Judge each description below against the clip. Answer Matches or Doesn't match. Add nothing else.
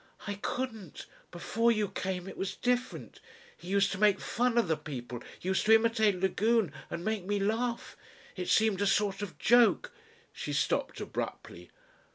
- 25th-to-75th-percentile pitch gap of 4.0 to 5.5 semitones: Doesn't match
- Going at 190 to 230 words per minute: Doesn't match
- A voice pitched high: Matches